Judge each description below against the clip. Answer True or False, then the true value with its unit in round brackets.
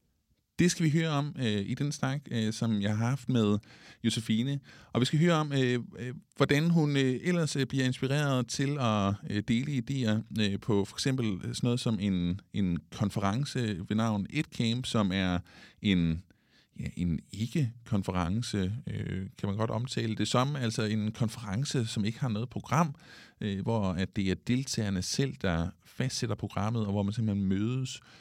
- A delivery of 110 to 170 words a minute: False (180 wpm)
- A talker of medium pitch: False (115 Hz)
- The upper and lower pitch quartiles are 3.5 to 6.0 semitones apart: True (4.4 semitones)